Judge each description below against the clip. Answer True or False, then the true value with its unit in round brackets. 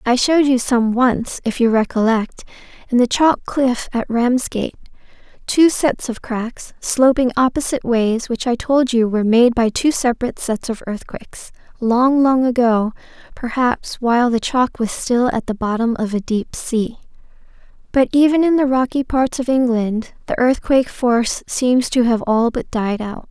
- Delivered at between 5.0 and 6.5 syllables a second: False (4.6 syllables/s)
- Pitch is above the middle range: True (245 Hz)